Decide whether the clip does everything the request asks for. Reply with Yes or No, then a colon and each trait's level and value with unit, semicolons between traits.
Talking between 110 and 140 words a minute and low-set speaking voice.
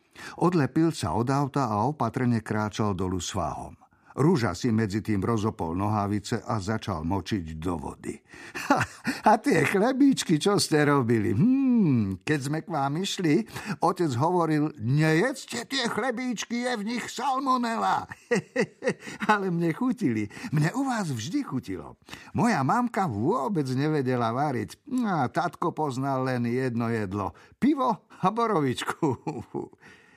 No: average, 130 wpm; medium, 145 Hz